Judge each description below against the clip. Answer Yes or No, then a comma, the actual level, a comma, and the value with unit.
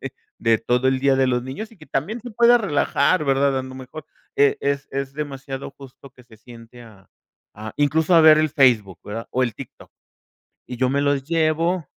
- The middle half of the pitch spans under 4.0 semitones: Yes, average, 3.5 semitones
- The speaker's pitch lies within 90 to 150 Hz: Yes, low, 135 Hz